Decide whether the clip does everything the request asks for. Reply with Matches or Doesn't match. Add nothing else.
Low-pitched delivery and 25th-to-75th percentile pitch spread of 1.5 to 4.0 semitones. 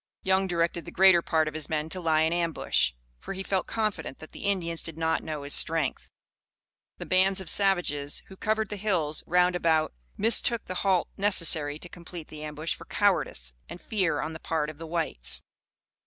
Doesn't match